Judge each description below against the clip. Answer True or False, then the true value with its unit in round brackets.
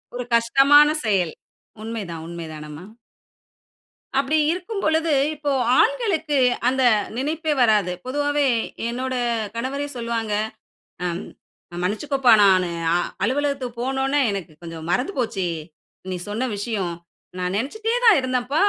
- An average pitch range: False (6.4 semitones)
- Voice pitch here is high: True (255 Hz)